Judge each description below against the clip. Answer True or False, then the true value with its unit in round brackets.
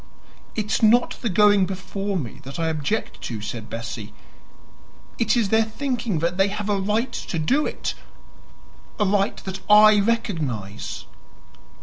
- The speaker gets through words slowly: False (150 wpm)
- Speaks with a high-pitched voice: True (200 Hz)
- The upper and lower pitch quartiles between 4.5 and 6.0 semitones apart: True (5.6 semitones)